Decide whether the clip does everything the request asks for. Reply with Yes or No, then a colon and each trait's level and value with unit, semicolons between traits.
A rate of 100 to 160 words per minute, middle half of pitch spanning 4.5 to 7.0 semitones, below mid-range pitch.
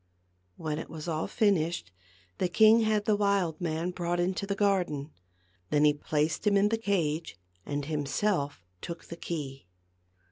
No: average, 155 wpm; average, 4.8 semitones; medium, 170 Hz